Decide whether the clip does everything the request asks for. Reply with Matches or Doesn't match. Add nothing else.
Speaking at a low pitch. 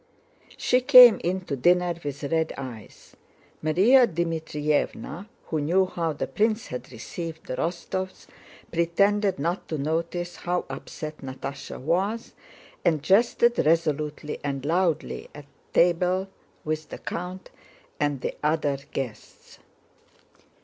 Doesn't match